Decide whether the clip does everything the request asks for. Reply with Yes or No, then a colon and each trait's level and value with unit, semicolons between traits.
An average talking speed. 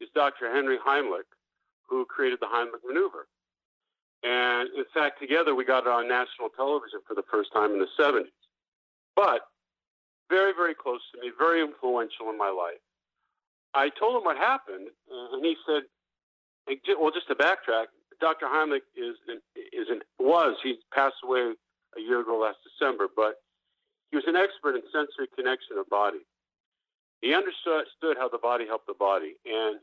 Yes: average, 165 wpm